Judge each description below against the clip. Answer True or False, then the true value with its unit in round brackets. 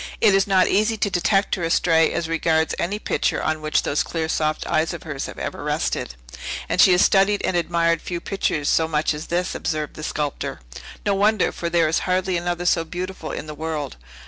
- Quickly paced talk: True (210 wpm)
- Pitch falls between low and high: True (170 Hz)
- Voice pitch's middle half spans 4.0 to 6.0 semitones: False (3.0 semitones)